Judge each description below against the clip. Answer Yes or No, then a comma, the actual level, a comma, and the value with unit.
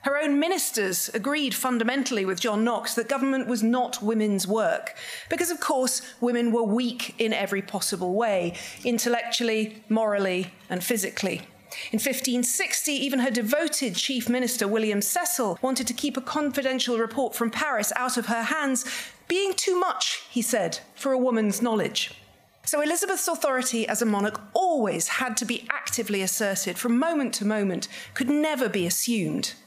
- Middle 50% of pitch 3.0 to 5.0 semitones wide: Yes, average, 4.0 semitones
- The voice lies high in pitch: Yes, high, 240 Hz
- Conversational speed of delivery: Yes, average, 160 wpm